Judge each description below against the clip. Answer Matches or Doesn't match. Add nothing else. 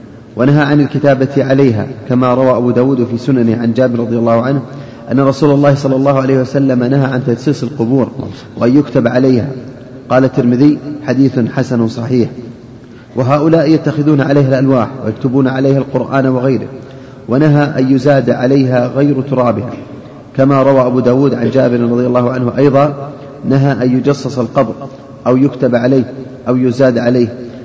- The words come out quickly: Matches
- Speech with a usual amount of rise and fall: Doesn't match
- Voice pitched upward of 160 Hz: Doesn't match